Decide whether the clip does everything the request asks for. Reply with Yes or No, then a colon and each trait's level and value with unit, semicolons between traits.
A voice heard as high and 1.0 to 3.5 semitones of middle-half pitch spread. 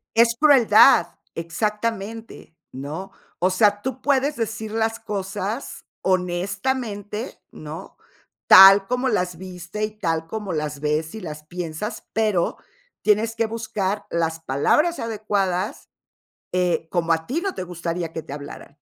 No: high, 195 Hz; average, 4.7 semitones